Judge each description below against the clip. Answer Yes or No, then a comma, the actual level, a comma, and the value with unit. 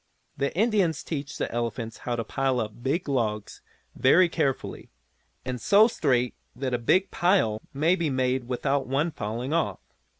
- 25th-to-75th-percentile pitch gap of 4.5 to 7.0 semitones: Yes, average, 5.2 semitones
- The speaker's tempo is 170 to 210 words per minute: No, average, 160 wpm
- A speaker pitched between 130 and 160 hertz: Yes, low, 135 Hz